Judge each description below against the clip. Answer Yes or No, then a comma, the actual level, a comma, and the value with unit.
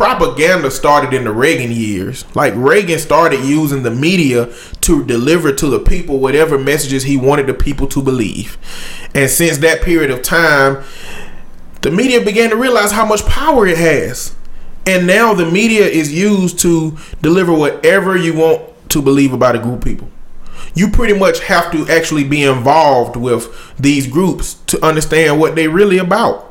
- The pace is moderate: Yes, average, 170 wpm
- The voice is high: No, medium, 155 Hz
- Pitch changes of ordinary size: Yes, average, 4.9 semitones